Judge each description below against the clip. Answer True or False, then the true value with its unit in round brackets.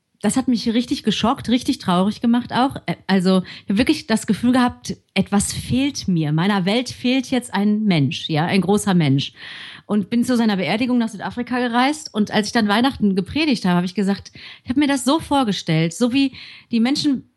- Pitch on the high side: True (220 Hz)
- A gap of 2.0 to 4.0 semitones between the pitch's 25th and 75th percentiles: False (4.5 semitones)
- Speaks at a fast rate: True (195 wpm)